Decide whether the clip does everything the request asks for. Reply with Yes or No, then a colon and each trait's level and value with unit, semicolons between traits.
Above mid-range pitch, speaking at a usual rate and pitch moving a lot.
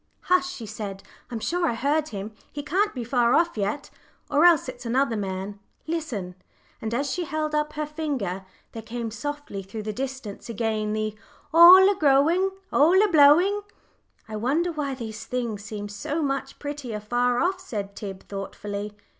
Yes: very high, 255 Hz; average, 170 wpm; wide, 6.3 semitones